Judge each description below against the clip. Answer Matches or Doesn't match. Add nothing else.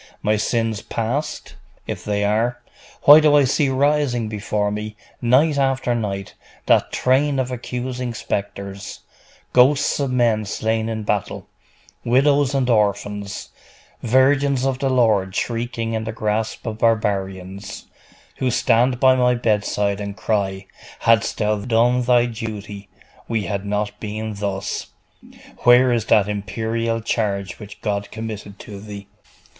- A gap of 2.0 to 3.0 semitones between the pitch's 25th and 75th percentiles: Doesn't match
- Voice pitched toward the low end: Matches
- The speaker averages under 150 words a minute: Matches